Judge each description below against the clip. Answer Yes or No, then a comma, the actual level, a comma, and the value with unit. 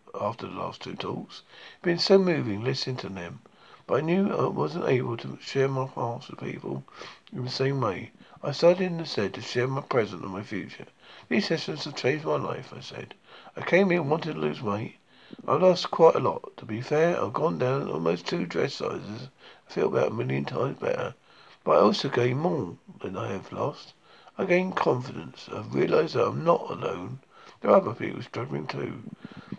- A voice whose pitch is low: No, medium, 145 Hz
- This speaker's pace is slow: No, fast, 205 wpm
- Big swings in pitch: Yes, wide, 6.2 semitones